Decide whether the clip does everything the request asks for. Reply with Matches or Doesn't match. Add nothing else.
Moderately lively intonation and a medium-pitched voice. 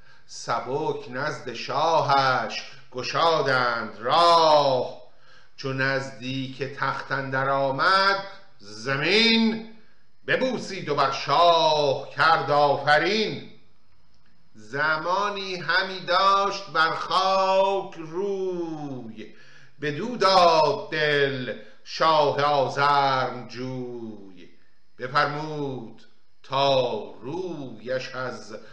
Doesn't match